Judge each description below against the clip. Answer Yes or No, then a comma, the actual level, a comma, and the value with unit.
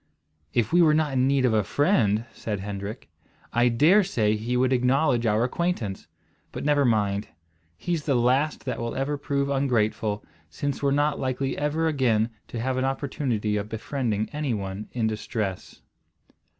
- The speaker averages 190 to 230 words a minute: No, average, 165 wpm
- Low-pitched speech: Yes, low, 125 Hz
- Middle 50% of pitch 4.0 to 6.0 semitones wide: Yes, average, 4.7 semitones